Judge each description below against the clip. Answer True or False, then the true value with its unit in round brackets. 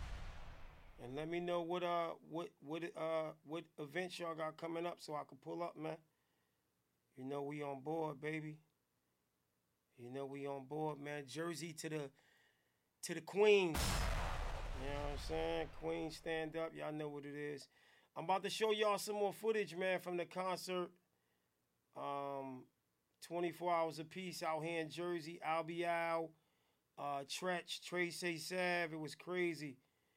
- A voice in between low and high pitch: True (160 Hz)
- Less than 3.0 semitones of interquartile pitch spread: False (3.8 semitones)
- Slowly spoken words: False (165 wpm)